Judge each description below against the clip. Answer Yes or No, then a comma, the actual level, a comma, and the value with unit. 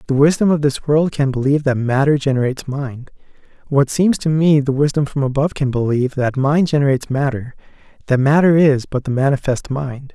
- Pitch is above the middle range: No, medium, 140 Hz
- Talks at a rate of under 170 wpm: No, average, 185 wpm